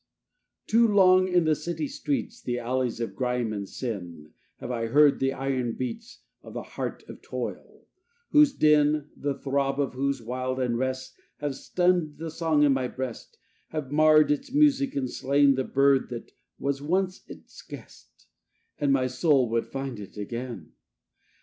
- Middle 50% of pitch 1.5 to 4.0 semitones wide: Yes, average, 3.6 semitones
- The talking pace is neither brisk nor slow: Yes, average, 170 wpm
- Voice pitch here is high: No, low, 135 Hz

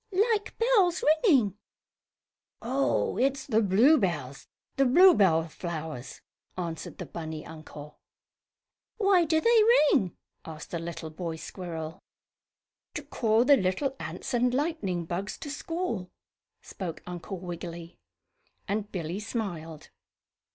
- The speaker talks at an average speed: No, slow, 115 wpm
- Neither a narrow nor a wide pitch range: No, wide, 8.7 semitones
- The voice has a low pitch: No, high, 195 Hz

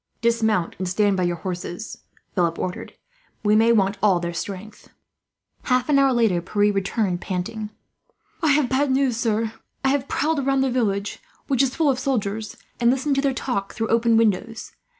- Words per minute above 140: Yes, average, 180 wpm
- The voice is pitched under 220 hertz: No, high, 225 Hz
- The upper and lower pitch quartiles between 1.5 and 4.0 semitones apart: No, average, 4.9 semitones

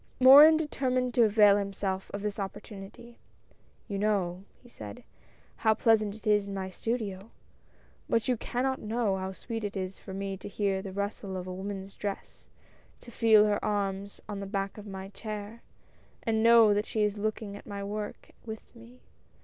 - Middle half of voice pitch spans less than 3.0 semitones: Yes, narrow, 2.4 semitones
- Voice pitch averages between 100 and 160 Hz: No, high, 205 Hz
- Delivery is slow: No, average, 175 wpm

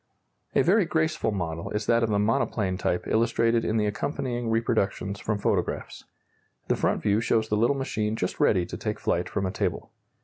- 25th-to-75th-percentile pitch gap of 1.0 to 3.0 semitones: Yes, narrow, 2.4 semitones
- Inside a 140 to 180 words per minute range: No, average, 190 wpm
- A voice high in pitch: No, low, 110 Hz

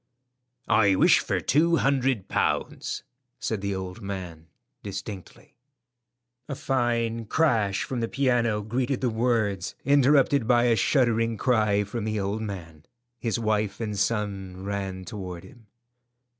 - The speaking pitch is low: Yes, low, 110 Hz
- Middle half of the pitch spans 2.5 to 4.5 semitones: Yes, average, 3.5 semitones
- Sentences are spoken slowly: Yes, slow, 130 wpm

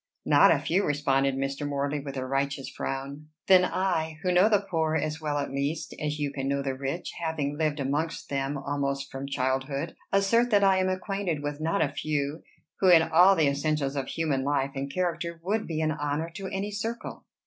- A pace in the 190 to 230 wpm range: Yes, fast, 205 wpm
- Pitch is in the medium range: Yes, medium, 150 Hz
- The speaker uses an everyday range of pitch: Yes, average, 3.6 semitones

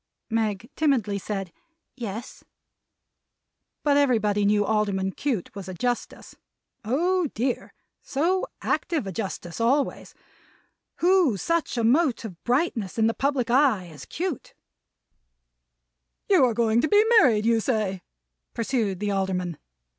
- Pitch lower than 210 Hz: No, high, 230 Hz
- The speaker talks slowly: Yes, slow, 125 wpm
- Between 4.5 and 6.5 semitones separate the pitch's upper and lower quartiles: Yes, wide, 5.6 semitones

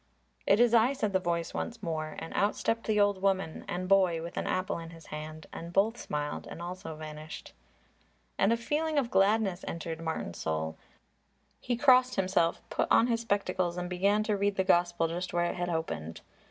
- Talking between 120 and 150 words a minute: No, average, 195 wpm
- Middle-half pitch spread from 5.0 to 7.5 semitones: No, average, 4.2 semitones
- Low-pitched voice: No, medium, 185 Hz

